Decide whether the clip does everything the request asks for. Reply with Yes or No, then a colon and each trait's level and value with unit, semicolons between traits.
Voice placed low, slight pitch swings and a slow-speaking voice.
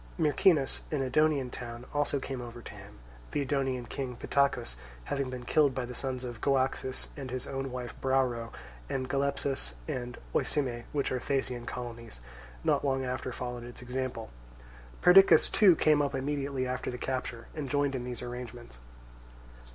No: low, 130 Hz; narrow, 2.2 semitones; average, 160 wpm